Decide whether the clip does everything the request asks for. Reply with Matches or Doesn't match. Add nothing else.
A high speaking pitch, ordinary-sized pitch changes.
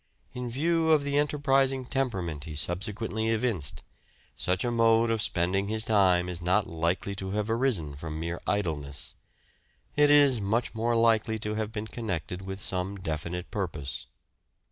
Doesn't match